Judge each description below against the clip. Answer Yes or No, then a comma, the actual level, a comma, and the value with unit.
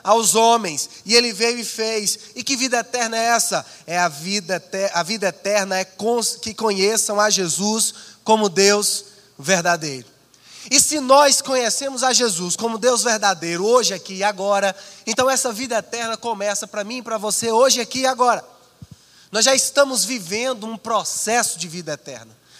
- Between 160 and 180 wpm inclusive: Yes, average, 165 wpm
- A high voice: Yes, high, 220 Hz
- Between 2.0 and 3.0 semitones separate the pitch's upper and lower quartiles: No, average, 3.4 semitones